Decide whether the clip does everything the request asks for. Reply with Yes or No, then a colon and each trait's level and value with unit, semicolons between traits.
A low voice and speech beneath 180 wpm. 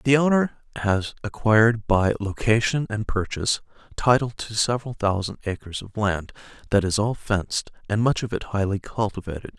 Yes: low, 110 Hz; average, 155 wpm